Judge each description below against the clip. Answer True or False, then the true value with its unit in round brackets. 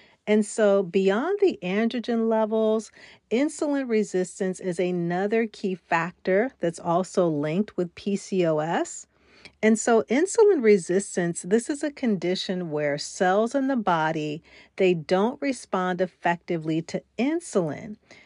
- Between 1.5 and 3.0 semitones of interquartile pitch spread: False (3.9 semitones)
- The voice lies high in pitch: True (200 Hz)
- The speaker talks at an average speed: False (120 wpm)